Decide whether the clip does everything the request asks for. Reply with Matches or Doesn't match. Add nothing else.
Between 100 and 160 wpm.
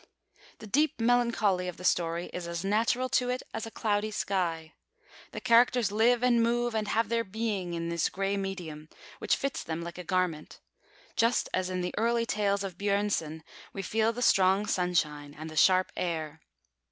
Doesn't match